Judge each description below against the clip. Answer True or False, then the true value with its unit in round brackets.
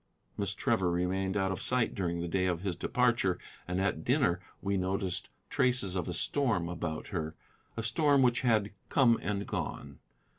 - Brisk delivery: False (175 wpm)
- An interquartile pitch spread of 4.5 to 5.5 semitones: True (4.8 semitones)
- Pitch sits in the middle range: False (95 Hz)